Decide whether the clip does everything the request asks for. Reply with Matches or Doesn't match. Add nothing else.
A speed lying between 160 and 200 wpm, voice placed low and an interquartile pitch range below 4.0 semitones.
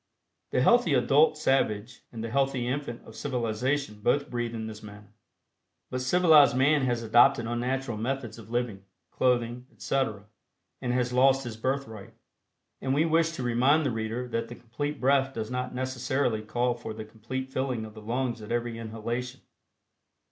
Matches